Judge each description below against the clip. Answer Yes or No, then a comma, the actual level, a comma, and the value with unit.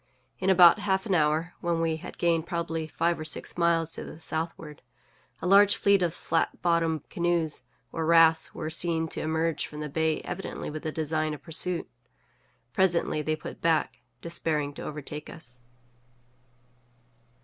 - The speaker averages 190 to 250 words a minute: No, average, 165 wpm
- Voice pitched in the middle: Yes, medium, 165 Hz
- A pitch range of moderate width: No, narrow, 1.7 semitones